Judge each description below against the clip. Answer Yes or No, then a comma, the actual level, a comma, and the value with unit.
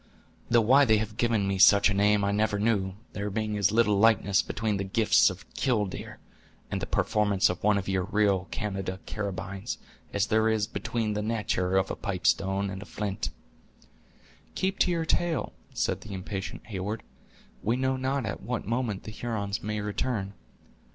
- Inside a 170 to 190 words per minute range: Yes, average, 180 wpm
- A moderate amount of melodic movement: No, narrow, 2.3 semitones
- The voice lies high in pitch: No, low, 105 Hz